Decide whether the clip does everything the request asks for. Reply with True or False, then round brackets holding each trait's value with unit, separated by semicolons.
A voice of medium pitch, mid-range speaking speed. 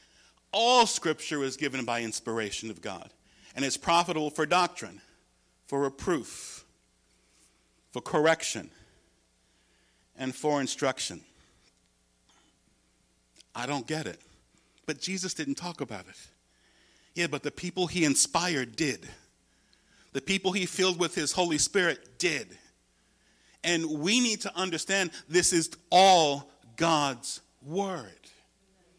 False (145 Hz; 115 wpm)